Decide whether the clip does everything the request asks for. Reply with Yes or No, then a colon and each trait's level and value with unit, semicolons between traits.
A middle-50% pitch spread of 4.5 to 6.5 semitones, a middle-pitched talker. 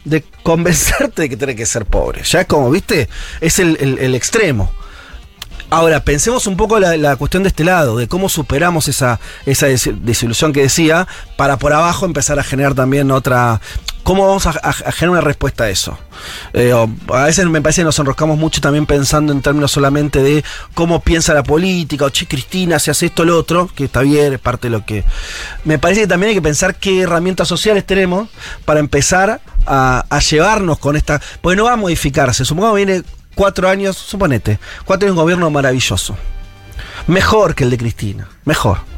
Yes: average, 5.1 semitones; medium, 150 Hz